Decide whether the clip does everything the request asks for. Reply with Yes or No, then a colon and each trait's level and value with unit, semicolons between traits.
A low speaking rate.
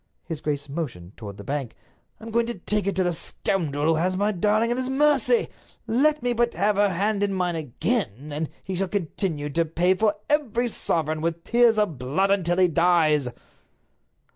No: average, 190 wpm